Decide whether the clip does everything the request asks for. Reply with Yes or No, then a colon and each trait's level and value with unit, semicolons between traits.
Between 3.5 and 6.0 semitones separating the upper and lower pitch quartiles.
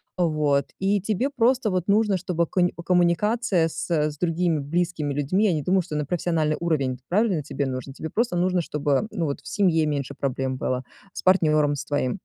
Yes: average, 4.2 semitones